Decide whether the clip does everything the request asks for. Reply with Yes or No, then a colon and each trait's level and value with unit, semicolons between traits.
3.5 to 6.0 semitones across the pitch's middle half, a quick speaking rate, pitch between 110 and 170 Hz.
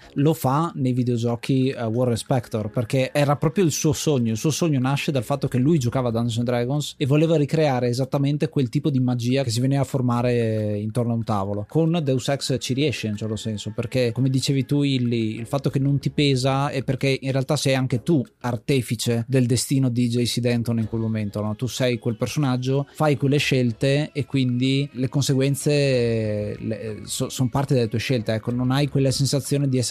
No: average, 2.8 semitones; fast, 210 wpm; low, 130 Hz